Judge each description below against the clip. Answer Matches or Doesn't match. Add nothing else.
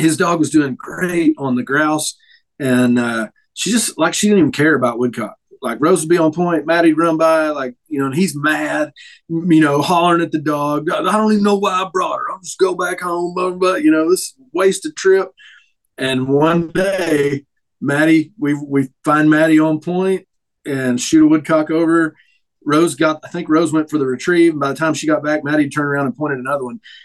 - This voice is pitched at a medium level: Matches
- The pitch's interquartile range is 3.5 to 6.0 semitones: Matches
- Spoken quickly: Matches